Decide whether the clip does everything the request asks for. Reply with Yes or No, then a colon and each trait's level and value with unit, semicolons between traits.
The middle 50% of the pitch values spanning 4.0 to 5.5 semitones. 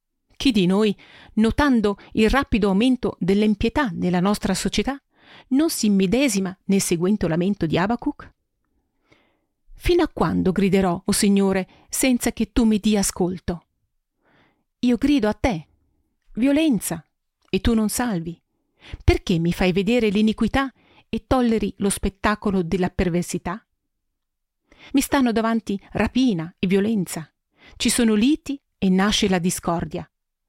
Yes: average, 4.4 semitones